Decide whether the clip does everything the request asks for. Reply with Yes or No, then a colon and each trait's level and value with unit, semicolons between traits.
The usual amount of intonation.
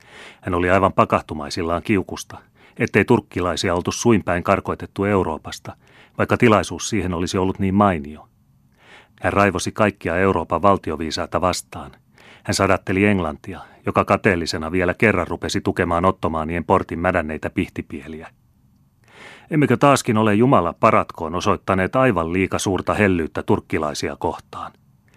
Yes: average, 3.1 semitones